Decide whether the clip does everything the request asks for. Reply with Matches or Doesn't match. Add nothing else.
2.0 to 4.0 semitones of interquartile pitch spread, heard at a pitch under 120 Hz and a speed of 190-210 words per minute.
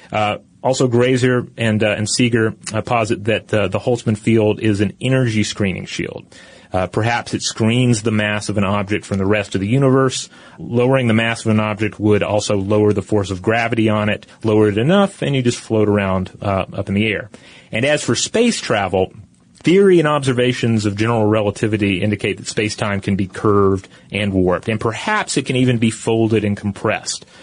Matches